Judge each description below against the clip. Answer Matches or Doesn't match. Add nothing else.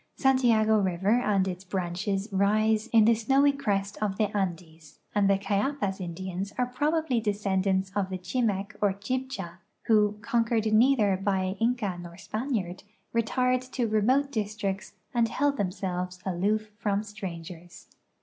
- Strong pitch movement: Doesn't match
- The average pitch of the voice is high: Matches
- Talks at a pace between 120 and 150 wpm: Matches